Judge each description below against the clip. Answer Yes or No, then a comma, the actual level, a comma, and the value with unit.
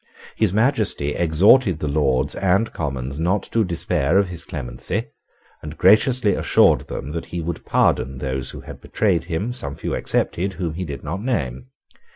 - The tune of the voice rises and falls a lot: Yes, wide, 5.9 semitones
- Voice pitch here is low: Yes, very low, 85 Hz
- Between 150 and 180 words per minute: Yes, average, 170 wpm